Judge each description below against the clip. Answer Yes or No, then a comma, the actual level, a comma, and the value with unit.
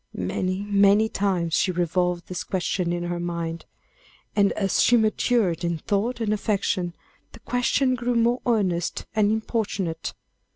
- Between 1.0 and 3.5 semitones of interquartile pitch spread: No, average, 4.0 semitones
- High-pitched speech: Yes, high, 195 Hz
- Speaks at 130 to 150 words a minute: Yes, average, 140 wpm